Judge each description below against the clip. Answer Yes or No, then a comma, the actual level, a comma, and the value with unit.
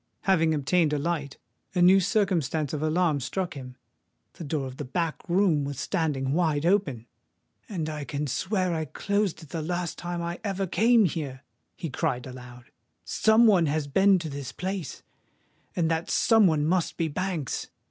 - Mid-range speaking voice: Yes, medium, 165 Hz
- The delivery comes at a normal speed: Yes, average, 175 wpm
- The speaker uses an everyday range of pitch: Yes, average, 4.3 semitones